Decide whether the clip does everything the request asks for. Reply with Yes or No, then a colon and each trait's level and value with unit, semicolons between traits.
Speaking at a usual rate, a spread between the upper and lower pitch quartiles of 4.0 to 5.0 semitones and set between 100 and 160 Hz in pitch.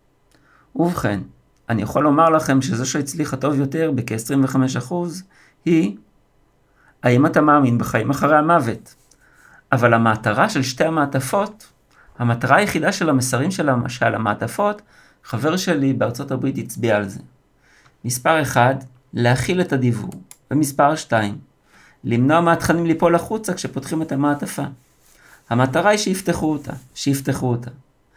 Yes: average, 120 wpm; average, 4.6 semitones; medium, 140 Hz